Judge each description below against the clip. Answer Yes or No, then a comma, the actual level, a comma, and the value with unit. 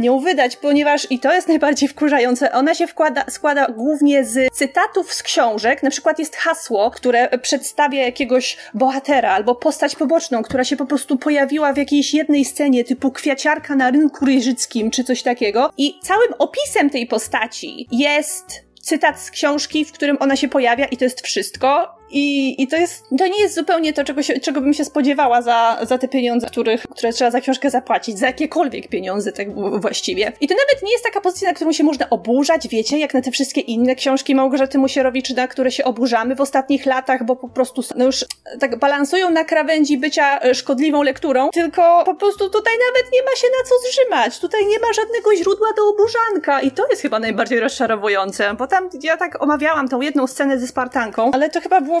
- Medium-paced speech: No, fast, 200 wpm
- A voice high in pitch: Yes, very high, 280 Hz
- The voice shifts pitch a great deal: No, average, 3.8 semitones